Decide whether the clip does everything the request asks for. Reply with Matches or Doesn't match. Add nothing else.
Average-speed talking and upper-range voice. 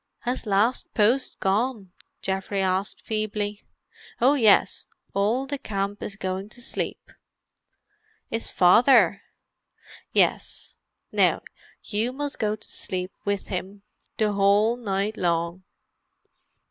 Doesn't match